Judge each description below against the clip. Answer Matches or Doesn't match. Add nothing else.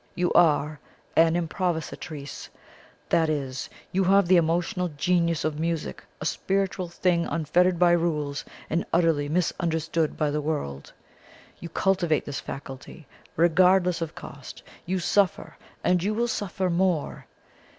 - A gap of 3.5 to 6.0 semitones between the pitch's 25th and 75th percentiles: Doesn't match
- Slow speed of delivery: Matches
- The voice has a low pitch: Doesn't match